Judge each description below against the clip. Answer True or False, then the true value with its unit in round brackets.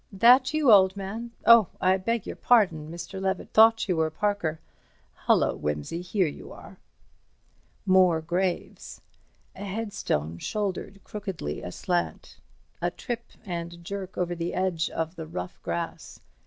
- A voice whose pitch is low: False (185 Hz)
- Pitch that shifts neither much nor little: True (3.5 semitones)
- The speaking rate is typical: False (130 wpm)